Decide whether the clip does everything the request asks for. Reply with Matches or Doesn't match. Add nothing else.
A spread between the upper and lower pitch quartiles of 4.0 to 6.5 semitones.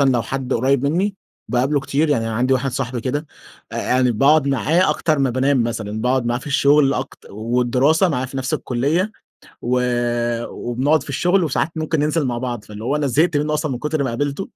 Doesn't match